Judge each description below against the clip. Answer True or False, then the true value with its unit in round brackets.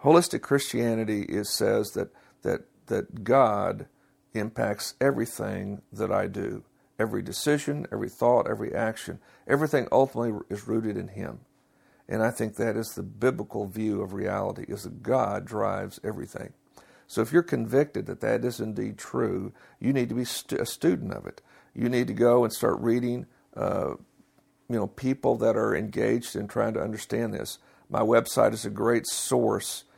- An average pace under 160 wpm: False (165 wpm)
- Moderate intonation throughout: True (3.3 semitones)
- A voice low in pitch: True (120 Hz)